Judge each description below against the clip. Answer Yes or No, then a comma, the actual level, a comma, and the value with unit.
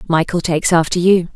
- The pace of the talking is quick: No, average, 175 wpm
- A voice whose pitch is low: No, medium, 170 Hz